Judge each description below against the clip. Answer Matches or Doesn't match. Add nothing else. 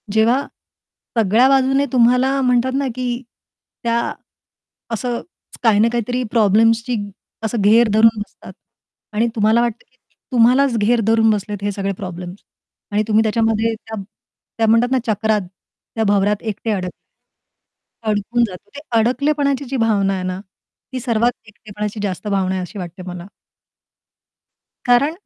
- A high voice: Matches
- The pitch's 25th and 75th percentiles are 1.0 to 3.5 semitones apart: Matches